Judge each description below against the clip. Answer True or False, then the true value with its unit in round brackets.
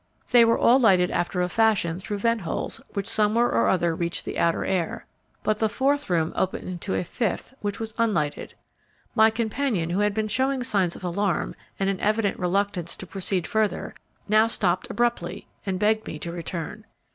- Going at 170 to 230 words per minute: True (185 wpm)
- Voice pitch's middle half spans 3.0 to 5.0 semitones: True (3.9 semitones)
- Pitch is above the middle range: True (200 Hz)